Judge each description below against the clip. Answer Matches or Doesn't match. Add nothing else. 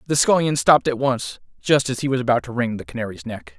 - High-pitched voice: Doesn't match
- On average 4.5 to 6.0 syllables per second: Doesn't match